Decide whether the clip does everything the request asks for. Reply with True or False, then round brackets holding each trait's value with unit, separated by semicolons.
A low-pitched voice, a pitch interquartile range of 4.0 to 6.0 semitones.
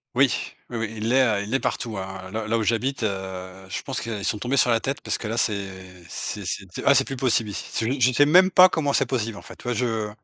True (115 Hz; 4.4 semitones)